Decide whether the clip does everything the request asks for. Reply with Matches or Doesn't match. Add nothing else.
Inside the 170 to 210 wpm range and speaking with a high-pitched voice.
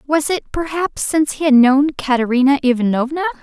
Doesn't match